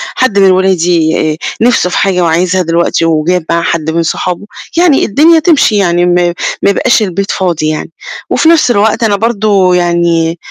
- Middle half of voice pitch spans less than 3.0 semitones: No, average, 3.8 semitones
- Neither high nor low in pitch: Yes, medium, 180 Hz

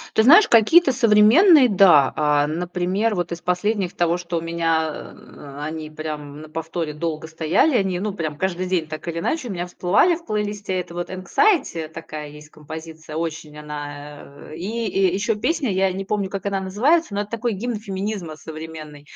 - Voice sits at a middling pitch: Yes, medium, 180 Hz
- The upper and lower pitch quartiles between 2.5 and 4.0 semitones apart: No, average, 5.0 semitones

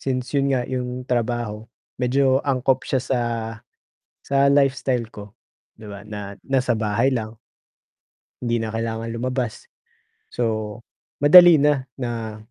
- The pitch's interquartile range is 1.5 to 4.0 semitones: Yes, average, 3.0 semitones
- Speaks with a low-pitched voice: Yes, low, 125 Hz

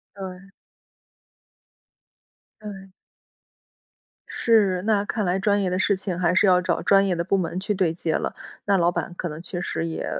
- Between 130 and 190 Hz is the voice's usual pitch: Yes, medium, 185 Hz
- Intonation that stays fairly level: Yes, narrow, 2.1 semitones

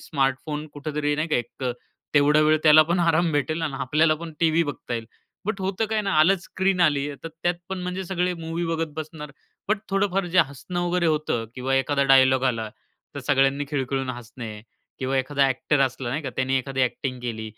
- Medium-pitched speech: Yes, medium, 150 Hz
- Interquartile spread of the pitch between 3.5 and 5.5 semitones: Yes, average, 4.1 semitones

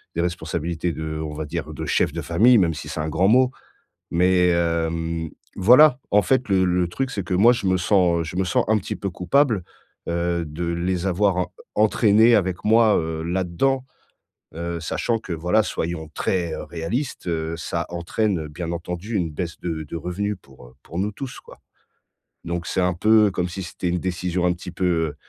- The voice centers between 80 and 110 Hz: Yes, very low, 90 Hz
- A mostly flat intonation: No, average, 3.2 semitones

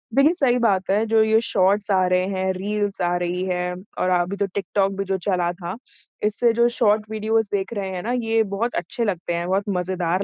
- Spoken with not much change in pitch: No, average, 3.1 semitones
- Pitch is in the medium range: No, high, 195 Hz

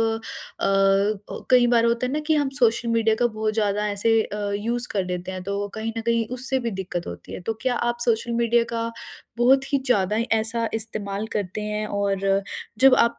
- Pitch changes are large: No, average, 2.7 semitones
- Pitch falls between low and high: No, high, 220 Hz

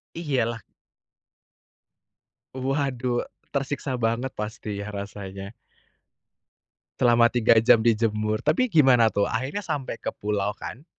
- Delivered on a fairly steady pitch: No, average, 3.7 semitones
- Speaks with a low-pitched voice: Yes, low, 120 Hz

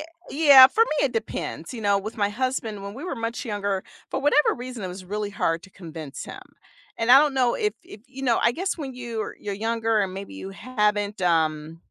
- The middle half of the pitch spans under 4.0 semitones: No, average, 4.7 semitones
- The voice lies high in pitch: Yes, high, 220 Hz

